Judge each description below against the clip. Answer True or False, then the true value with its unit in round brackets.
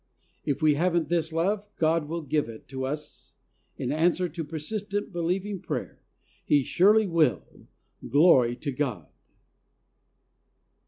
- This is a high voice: False (165 Hz)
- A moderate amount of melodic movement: True (3.5 semitones)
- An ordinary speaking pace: False (125 wpm)